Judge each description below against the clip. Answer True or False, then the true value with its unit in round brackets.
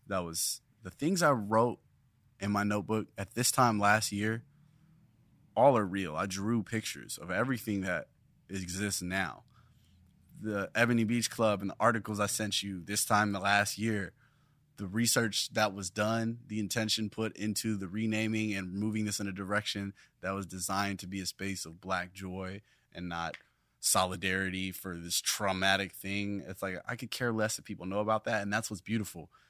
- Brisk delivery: False (180 wpm)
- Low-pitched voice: True (105 Hz)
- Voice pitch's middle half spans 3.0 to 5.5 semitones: False (2.5 semitones)